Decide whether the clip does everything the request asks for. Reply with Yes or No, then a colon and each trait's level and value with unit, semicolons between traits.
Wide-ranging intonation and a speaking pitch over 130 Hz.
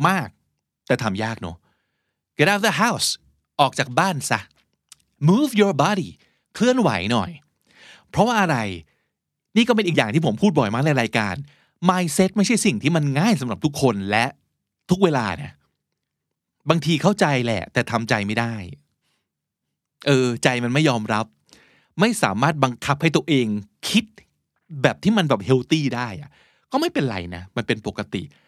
Yes: wide, 7.6 semitones; medium, 140 Hz